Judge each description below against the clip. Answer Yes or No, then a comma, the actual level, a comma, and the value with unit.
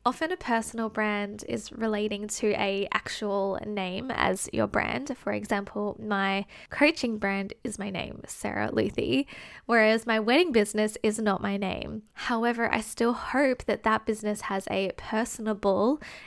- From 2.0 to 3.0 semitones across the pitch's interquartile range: Yes, narrow, 2.6 semitones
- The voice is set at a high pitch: Yes, high, 215 Hz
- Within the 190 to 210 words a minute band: No, average, 150 wpm